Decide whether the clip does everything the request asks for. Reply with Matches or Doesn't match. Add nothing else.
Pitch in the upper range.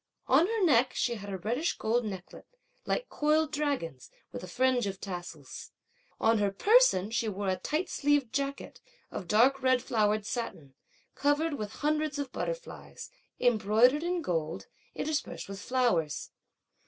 Matches